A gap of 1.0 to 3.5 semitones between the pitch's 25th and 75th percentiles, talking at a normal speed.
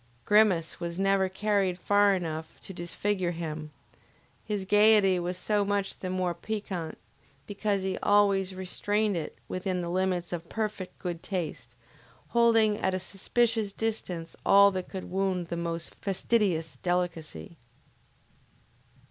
No: average, 2.7 semitones; slow, 130 wpm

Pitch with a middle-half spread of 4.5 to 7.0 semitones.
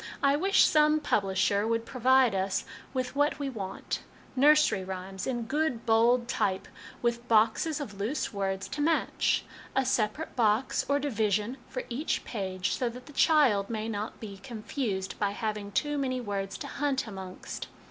Yes: average, 5.0 semitones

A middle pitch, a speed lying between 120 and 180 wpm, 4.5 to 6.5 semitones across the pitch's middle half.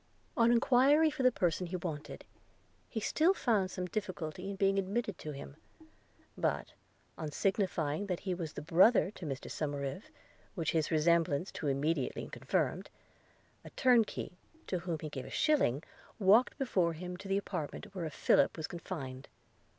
Yes: medium, 180 Hz; average, 155 wpm; average, 4.8 semitones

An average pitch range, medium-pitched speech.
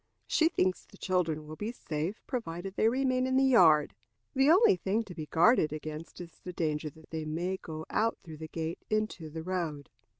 No: wide, 5.8 semitones; medium, 175 Hz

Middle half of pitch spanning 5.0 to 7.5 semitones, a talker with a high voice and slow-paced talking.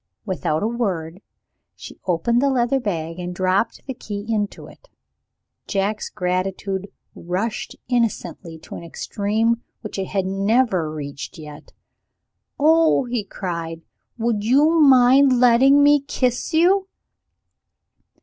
Yes: wide, 5.5 semitones; high, 210 Hz; slow, 120 wpm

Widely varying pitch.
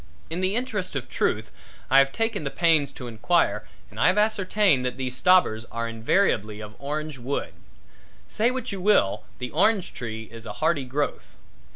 Yes: wide, 8.1 semitones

